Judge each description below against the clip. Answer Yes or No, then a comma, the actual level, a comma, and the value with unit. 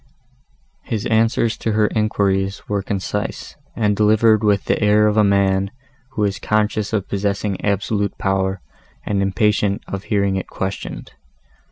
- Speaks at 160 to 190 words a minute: No, average, 145 wpm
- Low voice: Yes, low, 100 Hz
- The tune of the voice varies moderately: No, narrow, 1.5 semitones